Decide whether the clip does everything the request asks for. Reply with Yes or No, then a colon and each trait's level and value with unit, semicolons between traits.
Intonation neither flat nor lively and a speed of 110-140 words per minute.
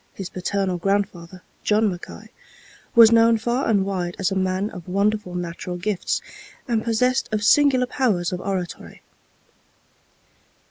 Yes: average, 3.7 semitones; slow, 135 wpm